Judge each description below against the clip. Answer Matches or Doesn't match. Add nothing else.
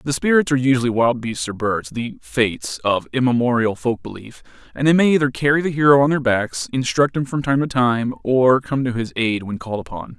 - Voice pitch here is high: Doesn't match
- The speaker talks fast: Matches